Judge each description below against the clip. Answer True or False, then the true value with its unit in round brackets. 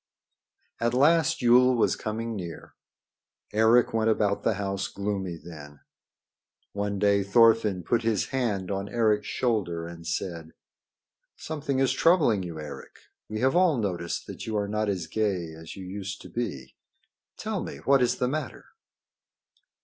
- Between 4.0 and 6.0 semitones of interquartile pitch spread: True (4.4 semitones)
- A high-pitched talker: False (105 Hz)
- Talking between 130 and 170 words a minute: True (150 wpm)